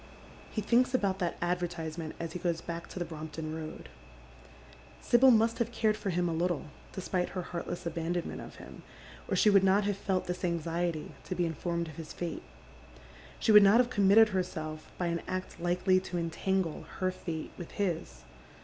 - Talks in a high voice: No, medium, 175 Hz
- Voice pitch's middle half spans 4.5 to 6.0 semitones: No, average, 2.7 semitones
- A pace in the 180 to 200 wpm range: Yes, average, 185 wpm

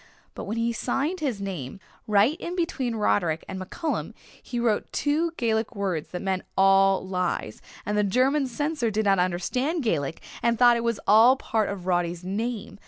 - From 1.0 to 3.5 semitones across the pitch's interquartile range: No, average, 4.7 semitones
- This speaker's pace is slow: No, average, 175 wpm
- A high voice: Yes, high, 215 Hz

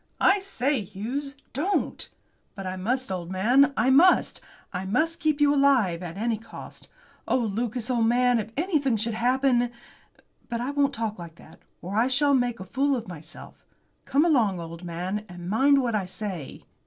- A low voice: No, high, 235 Hz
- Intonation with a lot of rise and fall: Yes, wide, 6.0 semitones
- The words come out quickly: No, average, 180 wpm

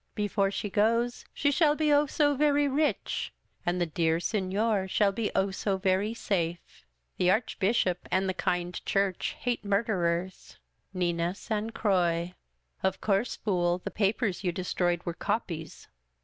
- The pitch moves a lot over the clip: No, average, 4.1 semitones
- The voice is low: No, high, 195 Hz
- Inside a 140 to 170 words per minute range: Yes, average, 155 wpm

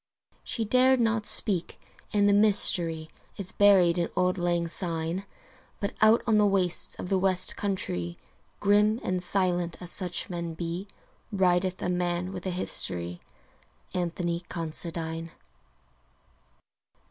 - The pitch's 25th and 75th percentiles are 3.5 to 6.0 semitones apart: No, average, 2.8 semitones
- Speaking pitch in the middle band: Yes, medium, 180 Hz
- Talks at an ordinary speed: No, slow, 130 wpm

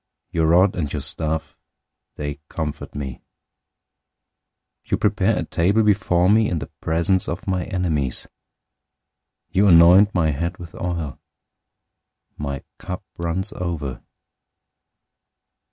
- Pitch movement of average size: Yes, average, 3.5 semitones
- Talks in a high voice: No, very low, 85 Hz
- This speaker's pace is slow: Yes, slow, 120 wpm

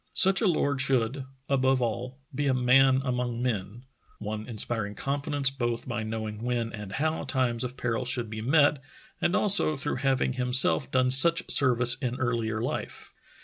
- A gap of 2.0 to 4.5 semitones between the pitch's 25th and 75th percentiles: Yes, average, 2.7 semitones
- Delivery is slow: No, average, 170 wpm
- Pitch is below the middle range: Yes, low, 125 Hz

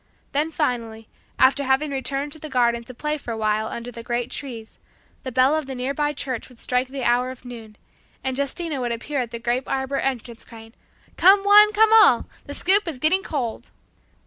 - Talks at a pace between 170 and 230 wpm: Yes, average, 200 wpm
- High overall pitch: Yes, very high, 260 Hz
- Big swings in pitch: No, average, 3.7 semitones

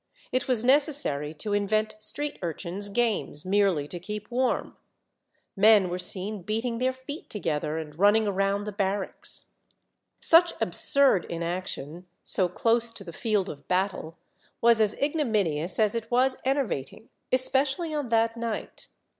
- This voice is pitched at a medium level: No, high, 210 Hz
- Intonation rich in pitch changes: No, average, 4.9 semitones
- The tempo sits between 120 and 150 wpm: Yes, average, 145 wpm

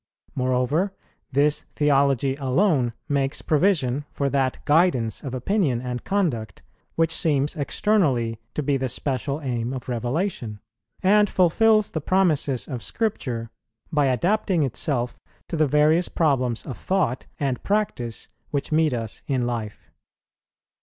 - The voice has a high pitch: No, medium, 140 Hz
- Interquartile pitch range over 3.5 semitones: Yes, average, 4.8 semitones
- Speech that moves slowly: Yes, slow, 130 wpm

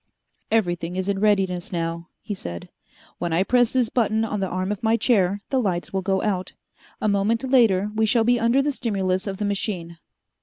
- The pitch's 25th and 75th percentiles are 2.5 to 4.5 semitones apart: Yes, average, 3.5 semitones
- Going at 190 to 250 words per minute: Yes, average, 200 wpm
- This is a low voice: No, high, 200 Hz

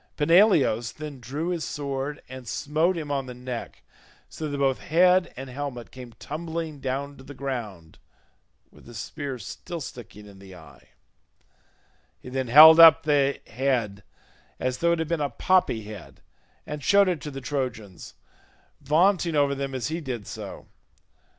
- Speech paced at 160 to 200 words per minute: Yes, average, 165 wpm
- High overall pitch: No, medium, 140 Hz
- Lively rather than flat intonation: No, average, 4.1 semitones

